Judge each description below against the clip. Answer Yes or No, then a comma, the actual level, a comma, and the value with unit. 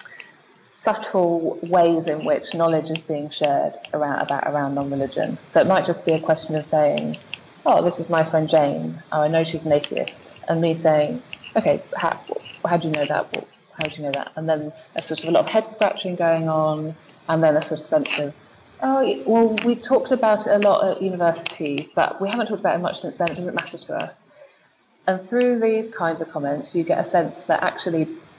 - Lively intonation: No, average, 3.7 semitones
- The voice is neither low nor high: Yes, medium, 165 Hz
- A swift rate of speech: Yes, fast, 220 wpm